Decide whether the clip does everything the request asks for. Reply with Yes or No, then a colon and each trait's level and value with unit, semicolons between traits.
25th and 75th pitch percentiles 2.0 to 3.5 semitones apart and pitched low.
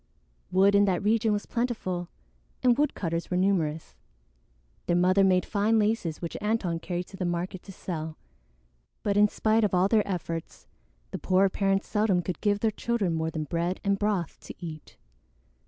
No: average, 3.1 semitones; high, 190 Hz